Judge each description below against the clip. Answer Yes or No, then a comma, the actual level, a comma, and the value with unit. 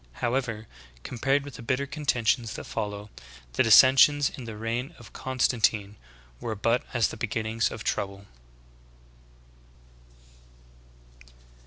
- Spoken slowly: Yes, slow, 125 wpm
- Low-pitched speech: Yes, low, 115 Hz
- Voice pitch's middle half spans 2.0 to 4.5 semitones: Yes, average, 3.3 semitones